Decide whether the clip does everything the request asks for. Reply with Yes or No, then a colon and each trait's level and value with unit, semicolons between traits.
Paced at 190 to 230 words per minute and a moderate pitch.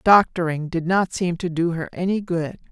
Yes: average, 200 wpm; medium, 175 Hz